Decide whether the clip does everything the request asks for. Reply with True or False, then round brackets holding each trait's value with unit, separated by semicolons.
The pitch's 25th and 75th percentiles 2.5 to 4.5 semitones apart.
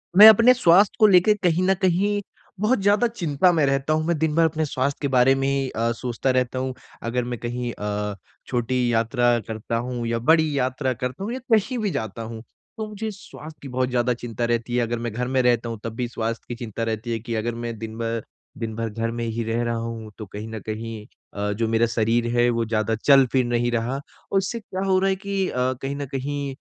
False (5.1 semitones)